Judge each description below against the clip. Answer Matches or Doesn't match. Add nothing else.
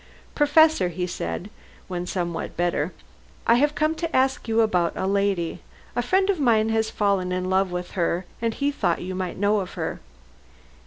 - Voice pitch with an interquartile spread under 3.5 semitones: Doesn't match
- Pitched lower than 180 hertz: Doesn't match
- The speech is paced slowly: Doesn't match